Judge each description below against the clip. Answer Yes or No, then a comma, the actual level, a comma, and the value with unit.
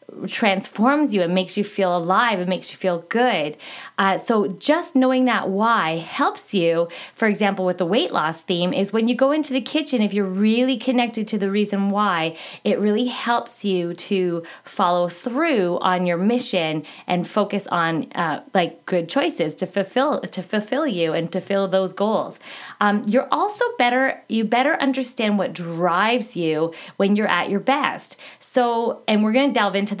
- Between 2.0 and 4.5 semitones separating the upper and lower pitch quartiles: No, average, 5.3 semitones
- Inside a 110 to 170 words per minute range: No, average, 180 wpm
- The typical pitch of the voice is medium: No, high, 205 Hz